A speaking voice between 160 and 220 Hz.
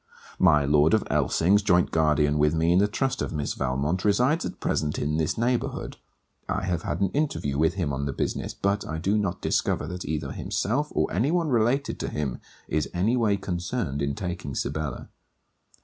No: very low, 85 Hz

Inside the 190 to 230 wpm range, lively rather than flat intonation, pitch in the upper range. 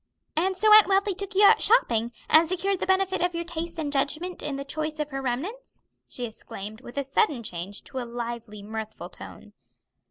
Yes: average, 200 wpm; wide, 7.8 semitones; very high, 300 Hz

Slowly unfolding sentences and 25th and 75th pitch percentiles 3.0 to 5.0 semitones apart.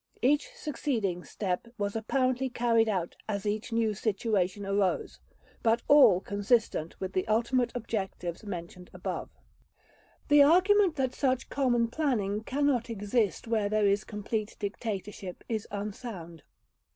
Yes: slow, 125 wpm; average, 3.8 semitones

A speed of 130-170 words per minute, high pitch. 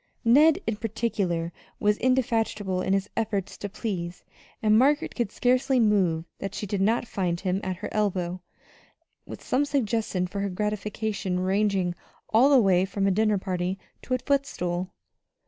Yes: average, 160 wpm; high, 205 Hz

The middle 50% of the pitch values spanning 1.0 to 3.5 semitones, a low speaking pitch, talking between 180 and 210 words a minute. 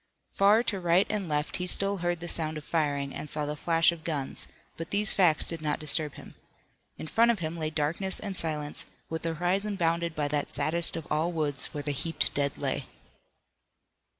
No: average, 2.9 semitones; medium, 165 Hz; fast, 205 wpm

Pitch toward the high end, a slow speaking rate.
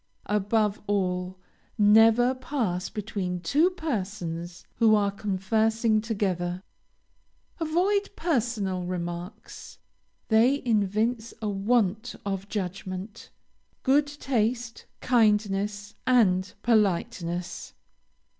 Yes: high, 210 Hz; slow, 80 wpm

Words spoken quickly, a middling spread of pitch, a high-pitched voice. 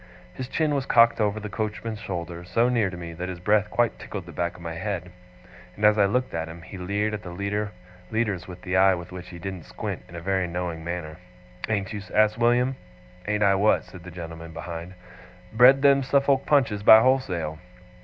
No: fast, 210 wpm; average, 4.1 semitones; low, 100 Hz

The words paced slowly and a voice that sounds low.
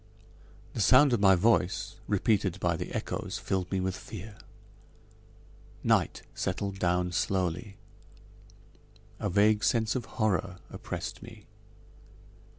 Yes: slow, 115 wpm; low, 100 Hz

